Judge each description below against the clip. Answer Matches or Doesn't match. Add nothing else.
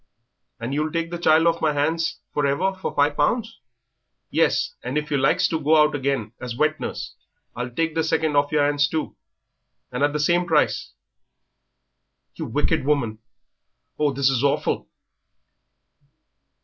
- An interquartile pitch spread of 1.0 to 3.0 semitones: Matches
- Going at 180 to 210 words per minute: Doesn't match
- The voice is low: Doesn't match